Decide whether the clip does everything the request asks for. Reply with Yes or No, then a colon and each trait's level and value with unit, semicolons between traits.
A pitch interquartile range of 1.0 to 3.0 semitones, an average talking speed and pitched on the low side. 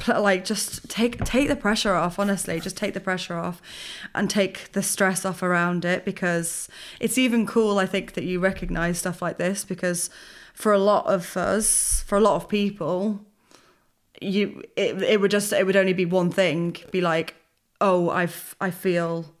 No: narrow, 2.5 semitones; average, 190 wpm; high, 190 Hz